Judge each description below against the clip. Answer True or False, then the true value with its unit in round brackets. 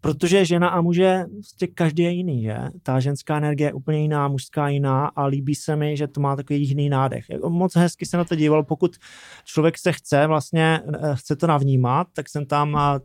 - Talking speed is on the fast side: True (205 wpm)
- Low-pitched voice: False (150 Hz)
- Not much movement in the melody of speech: False (3.3 semitones)